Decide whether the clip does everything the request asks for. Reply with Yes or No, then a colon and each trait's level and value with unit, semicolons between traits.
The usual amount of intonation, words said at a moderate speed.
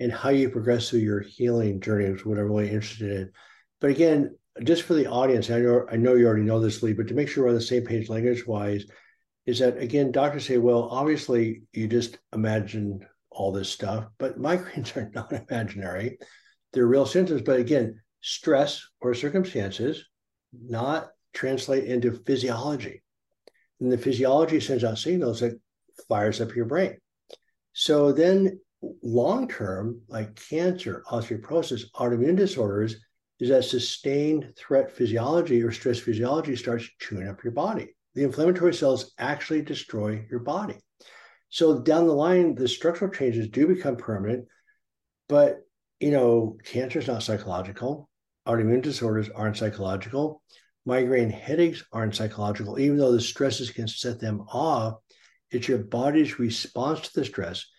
Yes: average, 4.2 semitones; average, 155 wpm